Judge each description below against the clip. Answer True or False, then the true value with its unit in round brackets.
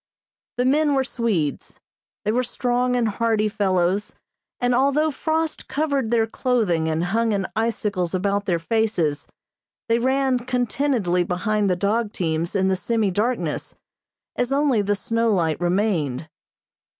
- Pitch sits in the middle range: False (220 Hz)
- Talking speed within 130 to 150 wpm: True (140 wpm)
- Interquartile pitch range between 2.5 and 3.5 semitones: False (5.1 semitones)